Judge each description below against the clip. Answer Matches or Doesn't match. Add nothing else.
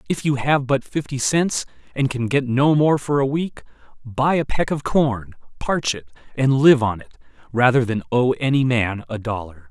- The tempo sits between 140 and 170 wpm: Doesn't match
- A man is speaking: Matches